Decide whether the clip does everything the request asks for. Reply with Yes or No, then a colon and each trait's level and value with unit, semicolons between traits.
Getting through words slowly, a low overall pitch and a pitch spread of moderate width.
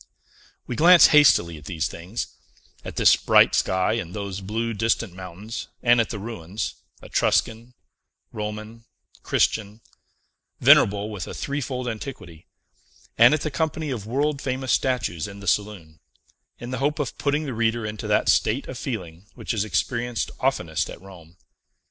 No: average, 155 wpm; low, 110 Hz; average, 4.6 semitones